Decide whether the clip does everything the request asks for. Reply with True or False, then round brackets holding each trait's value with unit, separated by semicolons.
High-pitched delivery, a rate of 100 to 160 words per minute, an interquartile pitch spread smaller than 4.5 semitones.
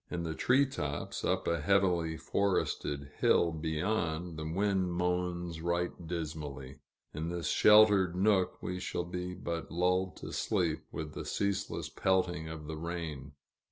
False (85 Hz; 145 wpm; 2.5 semitones)